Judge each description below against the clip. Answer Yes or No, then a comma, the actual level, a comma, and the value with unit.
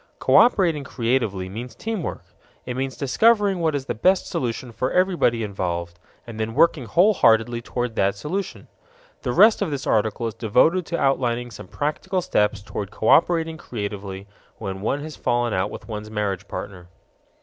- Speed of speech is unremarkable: Yes, average, 160 wpm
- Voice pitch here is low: Yes, low, 120 Hz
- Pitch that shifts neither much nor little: No, wide, 7.3 semitones